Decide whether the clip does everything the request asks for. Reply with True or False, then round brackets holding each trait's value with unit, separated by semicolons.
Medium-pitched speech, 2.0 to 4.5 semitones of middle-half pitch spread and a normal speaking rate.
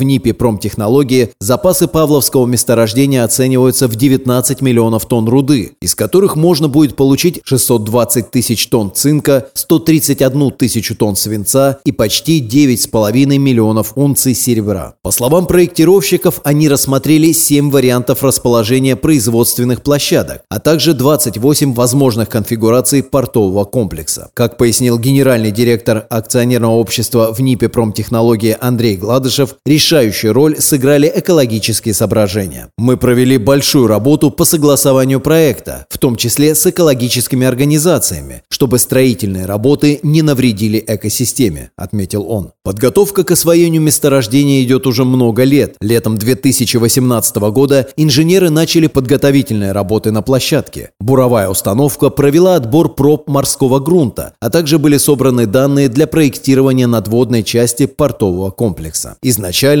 False (130 Hz; 4.0 semitones; 120 wpm)